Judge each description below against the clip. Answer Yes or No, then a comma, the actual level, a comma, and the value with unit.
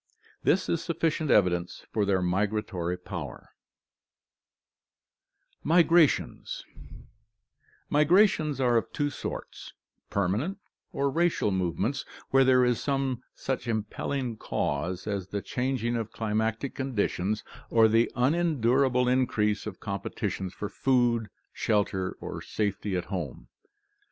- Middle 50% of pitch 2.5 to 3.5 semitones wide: No, average, 5.1 semitones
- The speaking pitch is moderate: No, low, 115 Hz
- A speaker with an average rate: No, slow, 115 wpm